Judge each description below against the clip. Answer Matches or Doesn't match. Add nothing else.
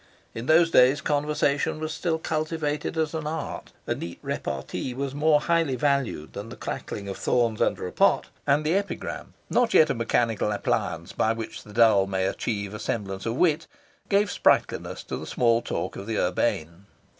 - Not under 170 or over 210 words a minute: Matches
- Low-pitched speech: Matches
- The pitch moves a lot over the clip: Matches